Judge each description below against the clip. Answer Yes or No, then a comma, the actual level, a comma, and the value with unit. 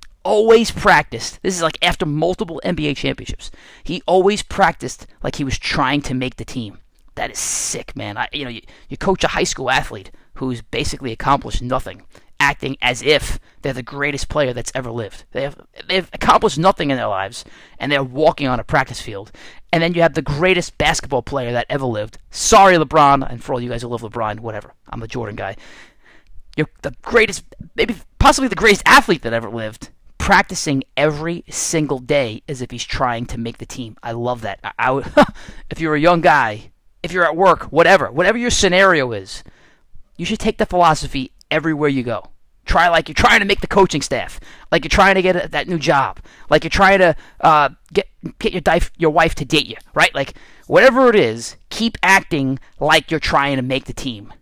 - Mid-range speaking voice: Yes, medium, 145 Hz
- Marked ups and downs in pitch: Yes, wide, 6.4 semitones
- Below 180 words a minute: No, fast, 205 wpm